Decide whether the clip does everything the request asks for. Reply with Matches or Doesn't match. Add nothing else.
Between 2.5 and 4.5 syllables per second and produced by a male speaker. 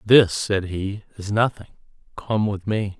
Matches